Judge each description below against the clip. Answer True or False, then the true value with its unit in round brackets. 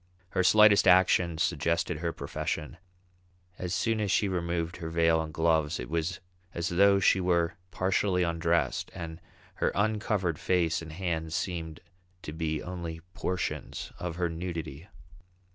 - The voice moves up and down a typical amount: False (2.1 semitones)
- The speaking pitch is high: False (85 Hz)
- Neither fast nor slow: True (145 wpm)